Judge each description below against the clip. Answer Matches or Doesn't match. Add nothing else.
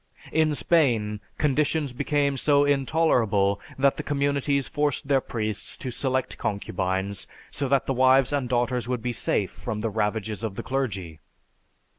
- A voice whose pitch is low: Matches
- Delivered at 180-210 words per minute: Doesn't match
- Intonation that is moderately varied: Matches